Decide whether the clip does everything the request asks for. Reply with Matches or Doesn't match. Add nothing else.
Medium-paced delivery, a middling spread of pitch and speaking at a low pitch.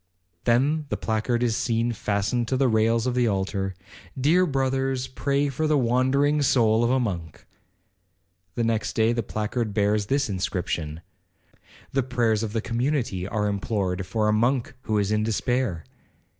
Matches